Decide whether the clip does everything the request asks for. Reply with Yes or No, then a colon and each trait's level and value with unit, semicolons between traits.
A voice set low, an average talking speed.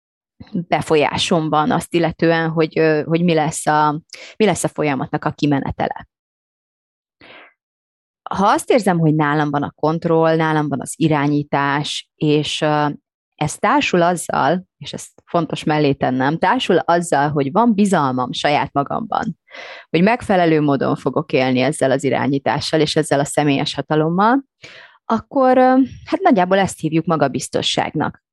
No: medium, 155 Hz; average, 130 wpm